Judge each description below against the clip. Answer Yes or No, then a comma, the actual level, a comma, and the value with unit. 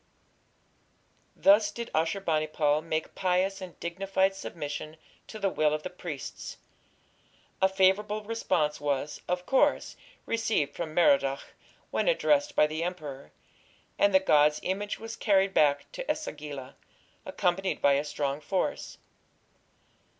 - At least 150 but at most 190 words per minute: No, slow, 135 wpm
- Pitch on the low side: No, medium, 180 Hz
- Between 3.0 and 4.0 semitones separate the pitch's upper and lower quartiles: No, average, 4.7 semitones